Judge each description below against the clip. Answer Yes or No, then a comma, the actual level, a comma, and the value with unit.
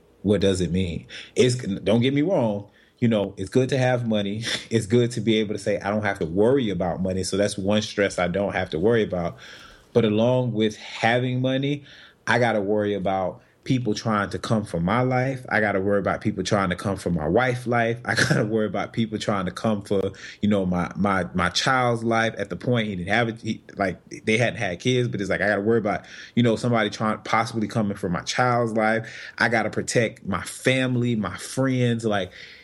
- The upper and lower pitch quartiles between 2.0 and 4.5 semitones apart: Yes, average, 3.2 semitones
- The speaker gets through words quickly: Yes, fast, 225 wpm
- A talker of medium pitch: No, low, 110 Hz